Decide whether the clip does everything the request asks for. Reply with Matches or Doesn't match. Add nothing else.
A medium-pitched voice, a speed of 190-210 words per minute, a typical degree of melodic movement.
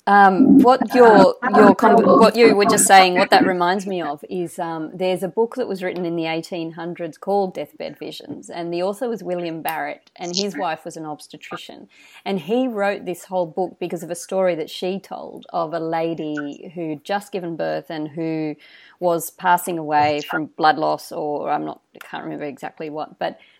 Matches